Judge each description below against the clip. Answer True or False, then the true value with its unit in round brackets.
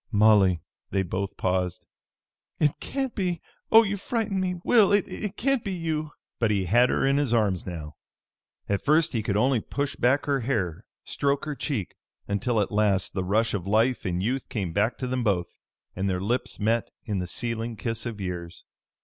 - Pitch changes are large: True (6.6 semitones)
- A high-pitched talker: False (115 Hz)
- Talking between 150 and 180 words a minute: False (190 wpm)